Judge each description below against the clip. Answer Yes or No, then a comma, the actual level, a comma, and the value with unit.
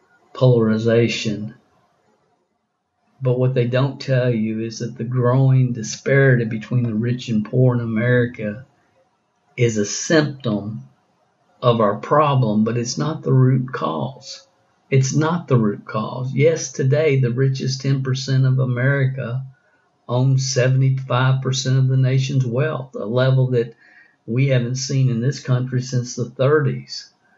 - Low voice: Yes, low, 130 Hz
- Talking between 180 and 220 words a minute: No, slow, 135 wpm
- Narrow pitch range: Yes, narrow, 2.0 semitones